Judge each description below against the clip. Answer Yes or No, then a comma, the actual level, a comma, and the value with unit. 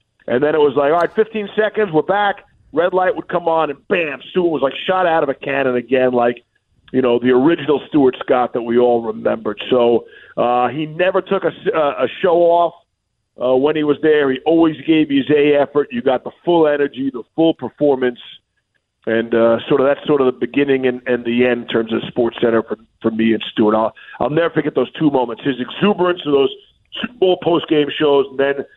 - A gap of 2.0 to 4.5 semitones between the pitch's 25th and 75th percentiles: No, wide, 5.4 semitones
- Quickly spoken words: Yes, fast, 225 wpm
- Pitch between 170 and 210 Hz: No, medium, 140 Hz